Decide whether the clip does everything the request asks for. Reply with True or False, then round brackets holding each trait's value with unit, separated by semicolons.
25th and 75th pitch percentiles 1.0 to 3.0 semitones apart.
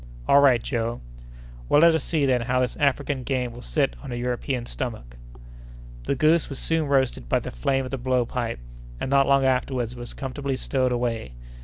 True (2.4 semitones)